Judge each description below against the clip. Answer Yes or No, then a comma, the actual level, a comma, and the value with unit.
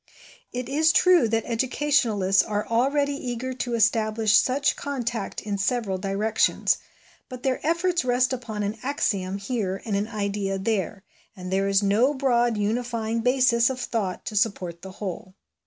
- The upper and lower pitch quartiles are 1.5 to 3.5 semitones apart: No, average, 4.1 semitones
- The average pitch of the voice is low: No, high, 225 Hz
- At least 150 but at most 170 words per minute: Yes, average, 155 wpm